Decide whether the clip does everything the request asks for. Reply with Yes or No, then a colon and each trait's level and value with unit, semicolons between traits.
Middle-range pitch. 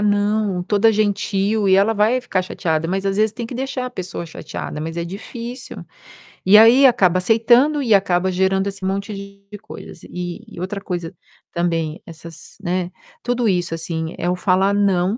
No: high, 195 Hz